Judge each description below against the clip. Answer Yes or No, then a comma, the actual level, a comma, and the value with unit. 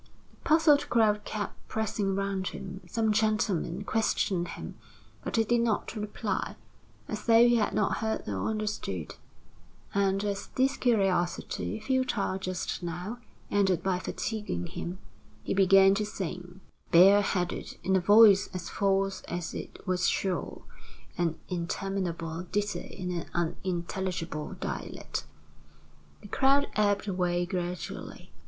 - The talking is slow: Yes, slow, 130 wpm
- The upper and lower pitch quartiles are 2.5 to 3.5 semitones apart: Yes, average, 3.0 semitones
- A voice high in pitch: Yes, high, 195 Hz